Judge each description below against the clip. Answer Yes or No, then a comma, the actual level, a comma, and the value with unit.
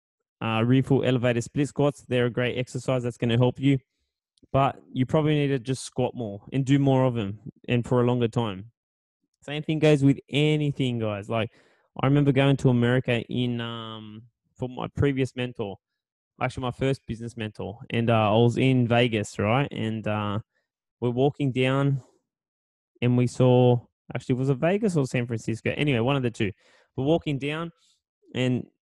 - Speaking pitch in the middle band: No, low, 125 Hz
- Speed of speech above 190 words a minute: No, average, 180 wpm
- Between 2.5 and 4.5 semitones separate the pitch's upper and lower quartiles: Yes, average, 3.0 semitones